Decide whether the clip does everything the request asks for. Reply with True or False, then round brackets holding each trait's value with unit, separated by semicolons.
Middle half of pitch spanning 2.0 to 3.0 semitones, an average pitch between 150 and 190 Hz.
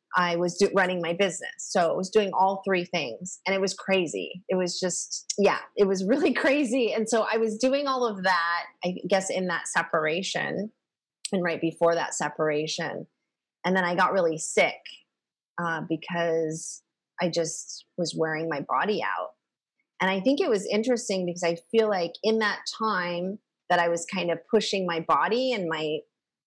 False (3.8 semitones; 185 Hz)